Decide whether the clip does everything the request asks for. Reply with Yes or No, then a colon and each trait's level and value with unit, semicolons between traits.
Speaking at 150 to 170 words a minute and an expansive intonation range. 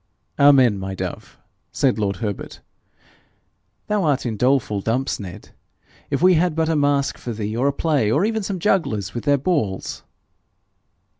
Yes: average, 155 wpm; wide, 7.0 semitones